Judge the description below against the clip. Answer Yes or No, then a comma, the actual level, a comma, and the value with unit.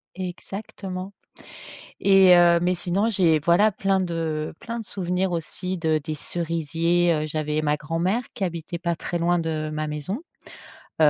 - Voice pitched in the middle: Yes, medium, 170 Hz